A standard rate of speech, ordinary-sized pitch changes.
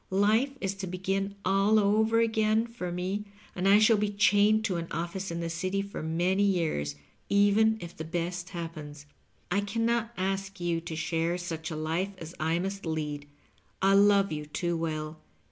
Yes: average, 185 wpm; average, 3.4 semitones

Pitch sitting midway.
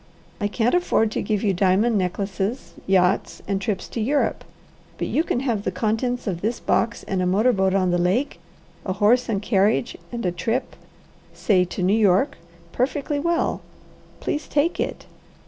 No: high, 210 Hz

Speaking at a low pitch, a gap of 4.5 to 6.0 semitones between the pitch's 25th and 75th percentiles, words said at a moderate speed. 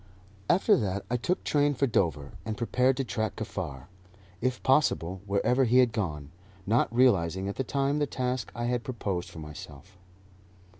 Yes: low, 115 Hz; wide, 5.5 semitones; average, 165 wpm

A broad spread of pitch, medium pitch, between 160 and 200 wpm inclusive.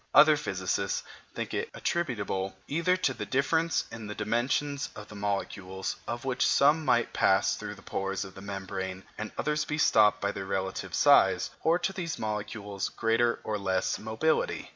No: wide, 6.9 semitones; low, 110 Hz; average, 170 wpm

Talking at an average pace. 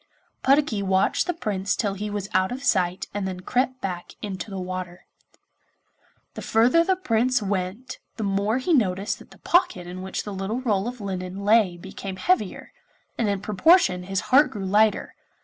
Yes: average, 180 wpm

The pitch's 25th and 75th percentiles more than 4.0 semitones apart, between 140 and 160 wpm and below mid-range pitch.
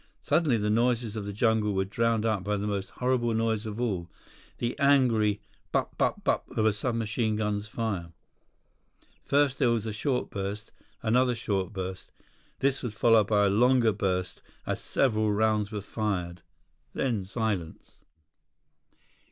No: narrow, 2.5 semitones; average, 150 wpm; low, 110 Hz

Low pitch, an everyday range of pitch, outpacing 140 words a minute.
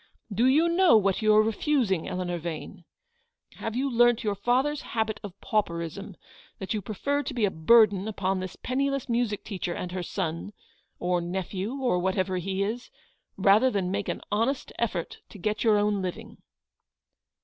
No: high, 205 Hz; average, 4.1 semitones; average, 170 wpm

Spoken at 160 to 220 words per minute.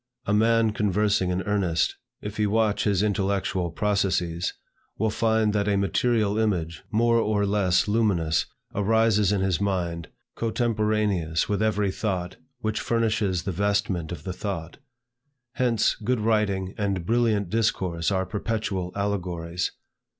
No: slow, 135 wpm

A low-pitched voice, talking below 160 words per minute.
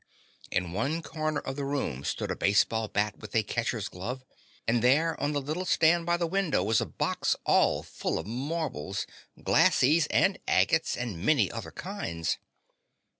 No: low, 130 Hz; average, 170 wpm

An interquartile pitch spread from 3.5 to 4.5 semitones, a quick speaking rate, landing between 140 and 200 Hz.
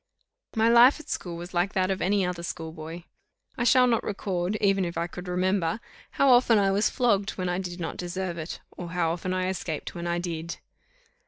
No: average, 2.7 semitones; fast, 215 wpm; medium, 185 Hz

